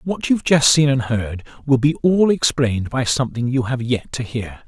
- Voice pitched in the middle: No, low, 130 Hz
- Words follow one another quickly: Yes, fast, 220 wpm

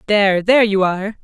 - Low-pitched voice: No, high, 205 Hz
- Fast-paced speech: No, average, 195 wpm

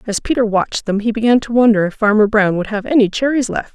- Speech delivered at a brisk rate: Yes, fast, 255 wpm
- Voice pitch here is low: No, high, 220 Hz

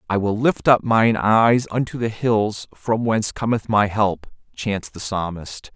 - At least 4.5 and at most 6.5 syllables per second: No, 4.0 syllables/s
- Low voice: Yes, low, 110 Hz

